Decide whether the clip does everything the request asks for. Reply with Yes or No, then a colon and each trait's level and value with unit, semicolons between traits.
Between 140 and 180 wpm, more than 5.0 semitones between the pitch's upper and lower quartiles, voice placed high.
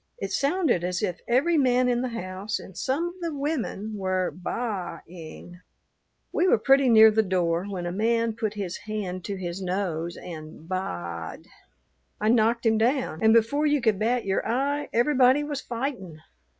Yes: average, 175 wpm; wide, 5.6 semitones; high, 220 Hz